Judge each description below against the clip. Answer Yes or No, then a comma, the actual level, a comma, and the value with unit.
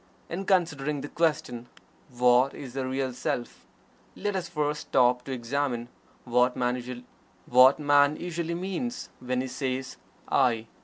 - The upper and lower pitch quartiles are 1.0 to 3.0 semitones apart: No, average, 3.6 semitones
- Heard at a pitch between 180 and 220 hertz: No, low, 135 Hz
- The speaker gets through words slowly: Yes, slow, 125 wpm